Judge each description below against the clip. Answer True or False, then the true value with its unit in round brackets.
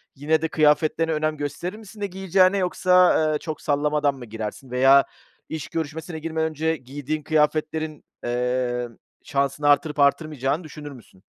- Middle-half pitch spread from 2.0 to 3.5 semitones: True (2.6 semitones)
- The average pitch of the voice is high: False (150 Hz)